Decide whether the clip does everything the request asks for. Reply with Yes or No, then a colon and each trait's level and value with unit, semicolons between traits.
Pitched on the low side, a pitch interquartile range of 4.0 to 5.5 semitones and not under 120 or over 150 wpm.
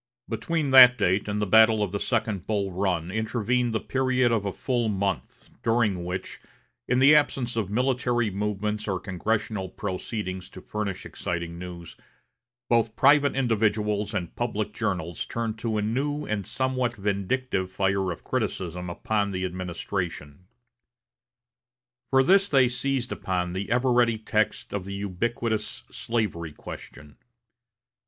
Yes: low, 105 Hz; average, 4.3 semitones; average, 140 wpm